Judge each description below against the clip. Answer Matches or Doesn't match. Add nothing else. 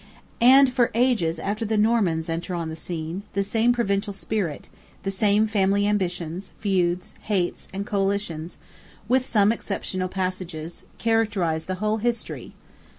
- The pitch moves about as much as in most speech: Matches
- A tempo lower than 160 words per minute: Matches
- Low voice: Doesn't match